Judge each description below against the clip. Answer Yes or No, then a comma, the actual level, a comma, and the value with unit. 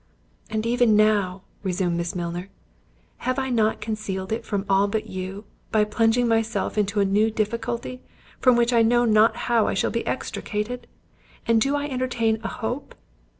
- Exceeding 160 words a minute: Yes, average, 170 wpm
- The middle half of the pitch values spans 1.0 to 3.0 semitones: Yes, average, 2.7 semitones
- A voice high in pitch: Yes, high, 220 Hz